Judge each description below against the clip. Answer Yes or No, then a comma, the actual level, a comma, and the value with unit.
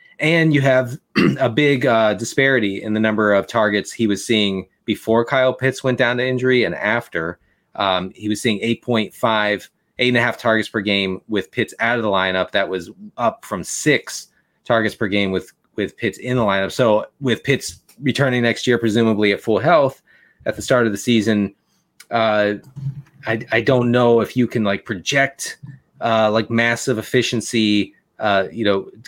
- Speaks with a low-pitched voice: Yes, low, 115 Hz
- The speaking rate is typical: Yes, average, 190 wpm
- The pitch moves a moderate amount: Yes, average, 3.4 semitones